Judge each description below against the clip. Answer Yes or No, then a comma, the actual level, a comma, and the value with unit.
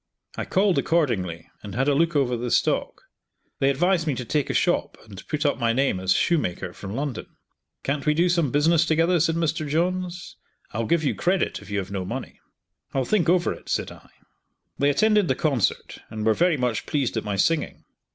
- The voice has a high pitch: No, medium, 145 Hz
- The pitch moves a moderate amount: No, wide, 6.2 semitones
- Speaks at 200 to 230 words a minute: Yes, fast, 205 wpm